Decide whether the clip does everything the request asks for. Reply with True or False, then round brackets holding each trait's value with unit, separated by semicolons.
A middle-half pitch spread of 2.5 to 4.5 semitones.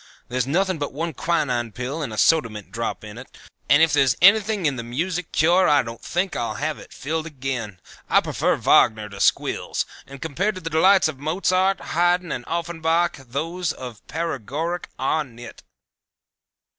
False (5.4 semitones)